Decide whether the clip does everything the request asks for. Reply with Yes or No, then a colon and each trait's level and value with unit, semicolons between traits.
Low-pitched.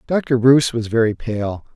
Yes: low, 120 Hz